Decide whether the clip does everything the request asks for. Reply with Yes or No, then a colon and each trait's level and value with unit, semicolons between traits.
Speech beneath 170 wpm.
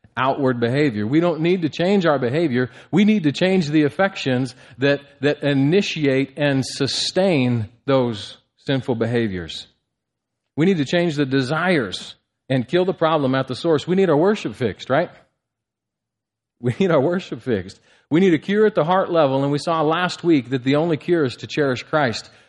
No: average, 180 wpm